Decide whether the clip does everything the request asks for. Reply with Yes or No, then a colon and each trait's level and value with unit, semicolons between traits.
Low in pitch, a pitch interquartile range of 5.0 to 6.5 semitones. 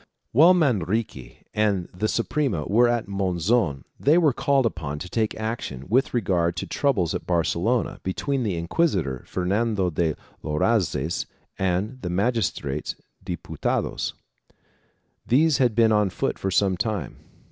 Yes: low, 100 Hz; wide, 5.4 semitones